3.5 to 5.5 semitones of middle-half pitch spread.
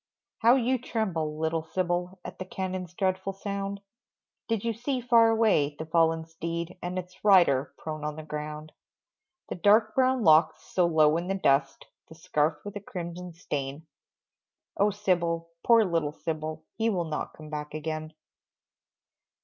Yes: average, 4.2 semitones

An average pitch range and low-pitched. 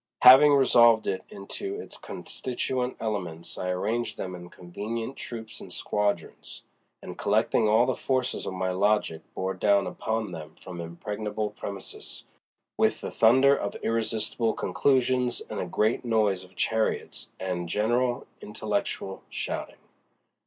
Yes: average, 4.3 semitones; low, 110 Hz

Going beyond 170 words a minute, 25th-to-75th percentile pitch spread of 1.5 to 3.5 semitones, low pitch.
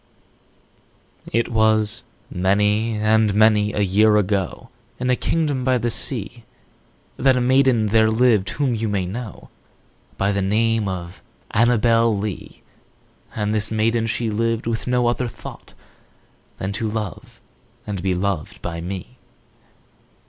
No: average, 140 wpm; narrow, 2.6 semitones; low, 110 Hz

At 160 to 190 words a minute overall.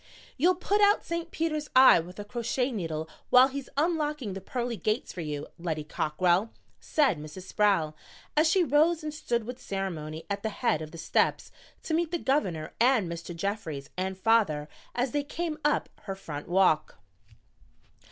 Yes: average, 170 wpm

